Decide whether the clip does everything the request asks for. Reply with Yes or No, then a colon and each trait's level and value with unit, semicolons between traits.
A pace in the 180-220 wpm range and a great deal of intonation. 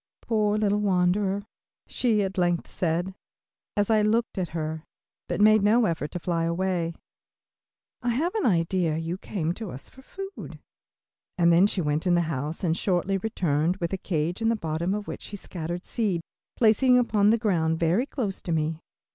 No: average, 185 wpm; average, 4.2 semitones